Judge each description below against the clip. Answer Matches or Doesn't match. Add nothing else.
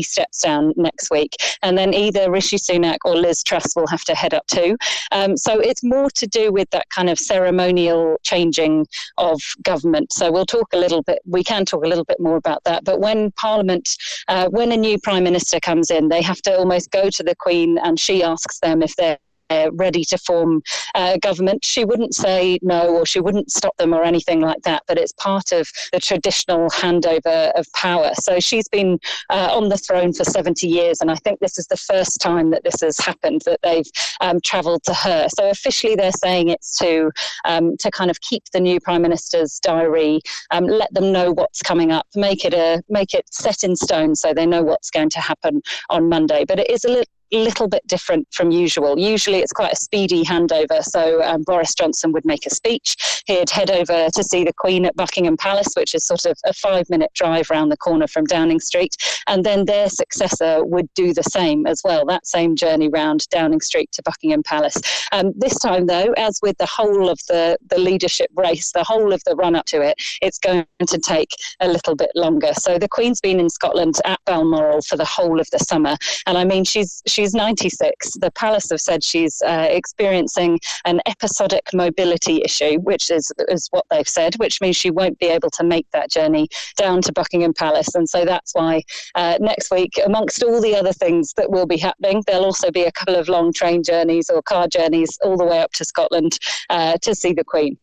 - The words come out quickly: Matches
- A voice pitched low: Doesn't match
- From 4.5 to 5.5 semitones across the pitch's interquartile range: Doesn't match